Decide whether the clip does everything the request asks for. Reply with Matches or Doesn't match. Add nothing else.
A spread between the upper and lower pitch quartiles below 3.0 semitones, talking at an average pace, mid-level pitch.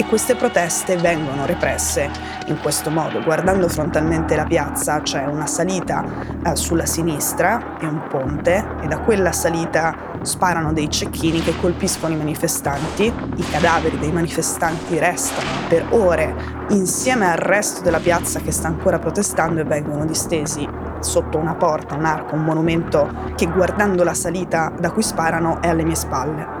Matches